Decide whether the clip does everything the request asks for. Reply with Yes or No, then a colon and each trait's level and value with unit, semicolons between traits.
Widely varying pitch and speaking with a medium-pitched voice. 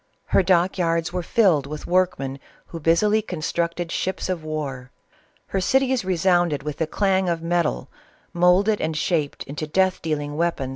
No: average, 3.2 semitones; medium, 170 Hz